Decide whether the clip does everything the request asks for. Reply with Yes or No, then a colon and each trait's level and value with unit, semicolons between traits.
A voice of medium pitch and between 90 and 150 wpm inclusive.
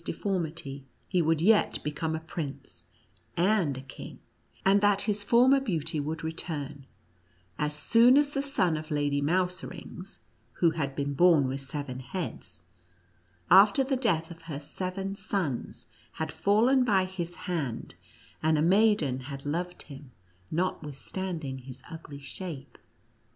Yes: medium, 165 Hz; average, 140 wpm